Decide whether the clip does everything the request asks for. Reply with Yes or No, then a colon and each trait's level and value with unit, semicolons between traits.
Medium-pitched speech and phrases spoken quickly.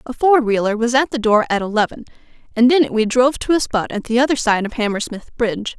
No: high, 235 Hz; fast, 250 wpm